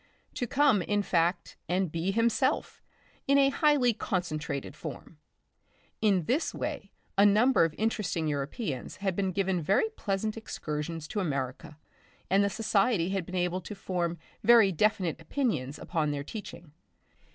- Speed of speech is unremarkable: Yes, average, 145 wpm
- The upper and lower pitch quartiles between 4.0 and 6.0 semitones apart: Yes, average, 4.8 semitones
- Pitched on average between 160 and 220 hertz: Yes, high, 190 Hz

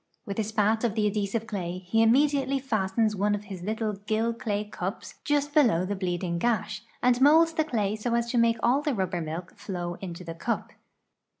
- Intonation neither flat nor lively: Yes, average, 3.7 semitones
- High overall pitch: Yes, high, 215 Hz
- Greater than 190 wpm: Yes, average, 200 wpm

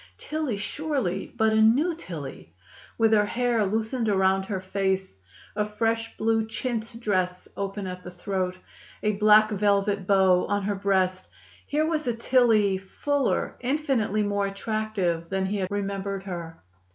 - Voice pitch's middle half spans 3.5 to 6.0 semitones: No, average, 2.8 semitones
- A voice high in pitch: Yes, high, 205 Hz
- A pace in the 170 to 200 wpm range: No, average, 150 wpm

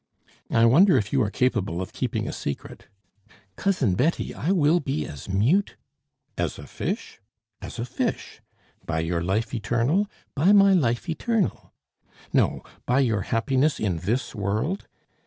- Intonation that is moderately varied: No, wide, 7.3 semitones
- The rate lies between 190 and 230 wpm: No, average, 155 wpm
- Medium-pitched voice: No, low, 125 Hz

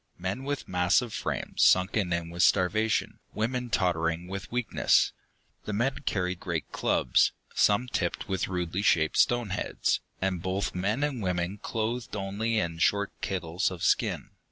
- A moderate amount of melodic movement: Yes, average, 3.8 semitones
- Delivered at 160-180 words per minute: No, average, 150 wpm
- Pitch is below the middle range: Yes, very low, 95 Hz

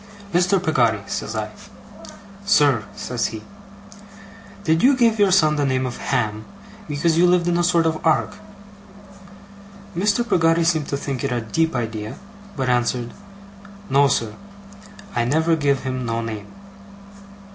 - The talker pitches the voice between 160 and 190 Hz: No, medium, 145 Hz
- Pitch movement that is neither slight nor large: No, wide, 6.0 semitones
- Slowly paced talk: No, average, 145 wpm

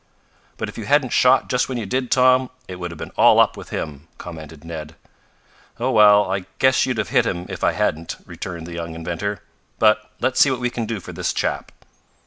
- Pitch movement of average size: No, wide, 6.9 semitones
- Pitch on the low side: Yes, low, 105 Hz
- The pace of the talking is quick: Yes, fast, 220 wpm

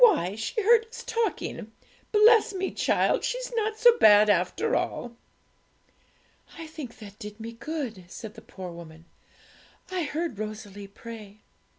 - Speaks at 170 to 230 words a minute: No, average, 145 wpm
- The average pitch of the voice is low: No, high, 235 Hz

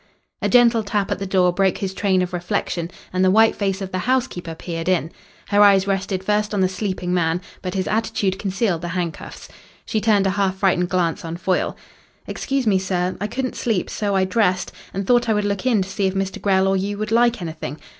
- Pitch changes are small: Yes, narrow, 2.2 semitones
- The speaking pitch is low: No, high, 195 Hz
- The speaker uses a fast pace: Yes, fast, 225 wpm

